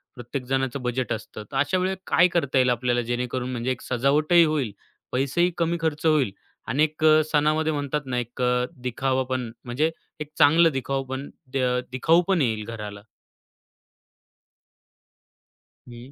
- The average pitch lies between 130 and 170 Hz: Yes, low, 135 Hz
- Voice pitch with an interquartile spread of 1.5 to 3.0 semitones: No, average, 3.7 semitones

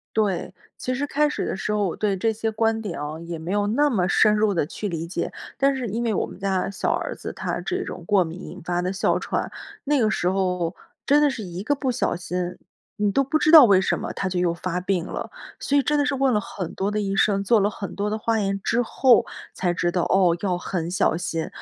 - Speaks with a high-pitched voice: Yes, high, 200 Hz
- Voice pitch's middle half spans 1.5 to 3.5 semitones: No, average, 4.1 semitones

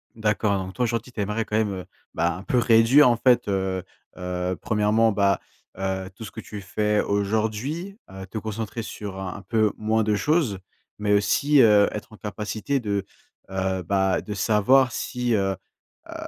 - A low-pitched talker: Yes, low, 105 Hz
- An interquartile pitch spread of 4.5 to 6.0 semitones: No, average, 2.8 semitones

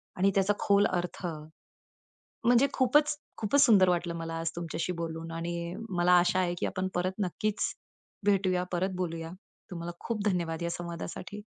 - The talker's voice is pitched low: No, medium, 180 Hz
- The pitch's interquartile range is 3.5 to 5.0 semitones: No, average, 2.8 semitones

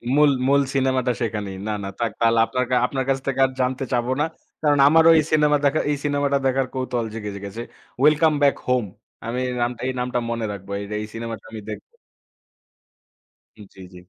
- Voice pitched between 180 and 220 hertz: No, low, 125 Hz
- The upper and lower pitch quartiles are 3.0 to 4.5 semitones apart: Yes, average, 3.7 semitones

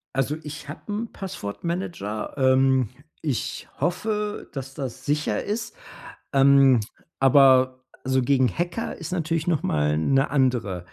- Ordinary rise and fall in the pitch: Yes, average, 4.5 semitones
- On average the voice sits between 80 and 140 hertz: Yes, low, 135 Hz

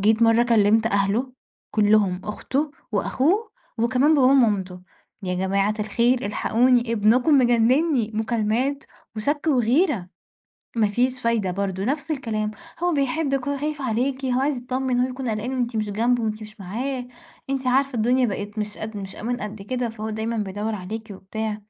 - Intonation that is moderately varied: Yes, average, 3.5 semitones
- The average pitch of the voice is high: Yes, high, 230 Hz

